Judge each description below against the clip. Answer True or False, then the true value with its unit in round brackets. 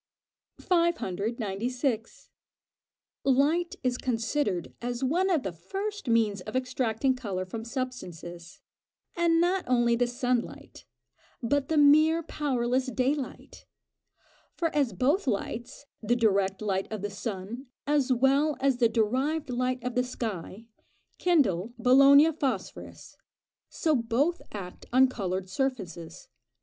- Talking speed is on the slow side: True (125 wpm)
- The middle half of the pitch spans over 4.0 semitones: True (4.9 semitones)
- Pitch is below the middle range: False (250 Hz)